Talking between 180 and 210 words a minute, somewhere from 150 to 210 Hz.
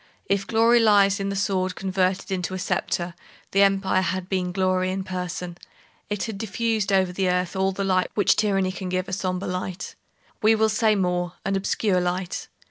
Yes: average, 185 wpm; high, 190 Hz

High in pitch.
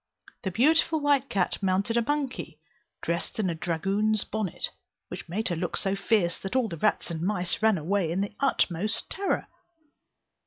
Yes: high, 200 Hz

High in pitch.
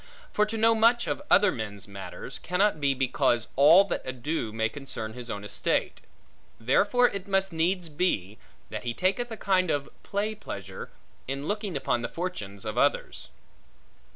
No: medium, 155 Hz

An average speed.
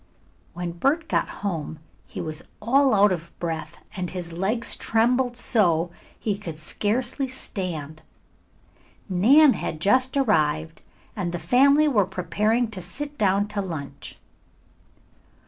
No: slow, 130 wpm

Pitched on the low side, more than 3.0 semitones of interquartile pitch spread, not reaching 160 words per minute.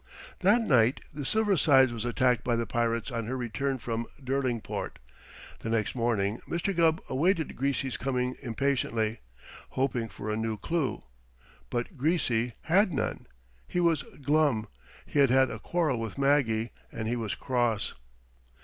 Yes: low, 130 Hz; average, 4.0 semitones; average, 150 wpm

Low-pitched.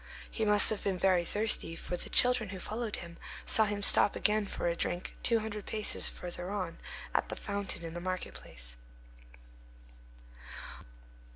No: high, 200 Hz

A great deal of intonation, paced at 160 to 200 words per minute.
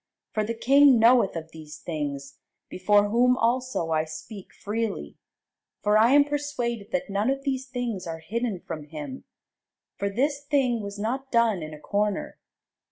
Yes: wide, 6.5 semitones; average, 165 wpm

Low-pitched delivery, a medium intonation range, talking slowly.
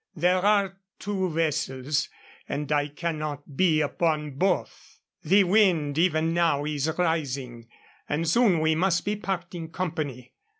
No: medium, 160 Hz; average, 3.8 semitones; slow, 130 wpm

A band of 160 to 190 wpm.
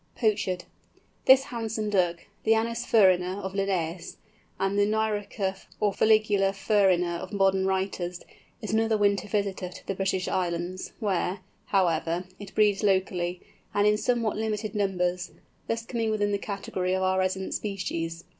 No: average, 145 wpm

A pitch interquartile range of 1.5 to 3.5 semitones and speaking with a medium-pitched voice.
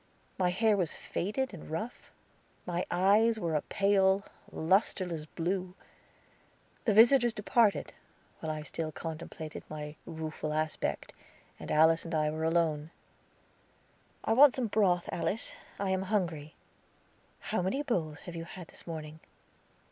No: average, 4.4 semitones; medium, 175 Hz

